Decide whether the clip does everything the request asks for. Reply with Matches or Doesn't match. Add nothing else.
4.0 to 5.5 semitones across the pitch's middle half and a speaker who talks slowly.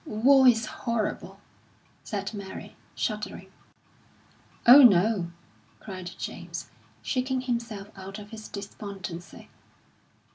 Doesn't match